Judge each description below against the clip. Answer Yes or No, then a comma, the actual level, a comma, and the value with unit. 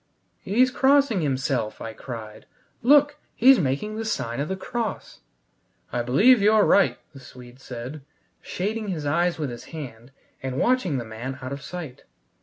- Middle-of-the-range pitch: Yes, medium, 150 Hz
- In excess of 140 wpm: Yes, average, 160 wpm